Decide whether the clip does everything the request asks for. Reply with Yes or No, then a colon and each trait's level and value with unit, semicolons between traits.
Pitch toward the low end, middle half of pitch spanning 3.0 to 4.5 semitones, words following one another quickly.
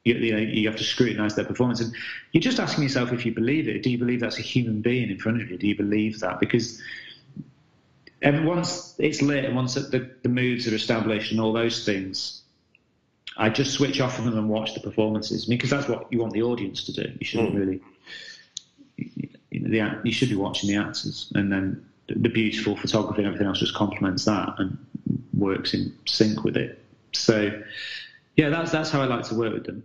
Yes: low, 115 Hz; average, 3.3 semitones; fast, 215 wpm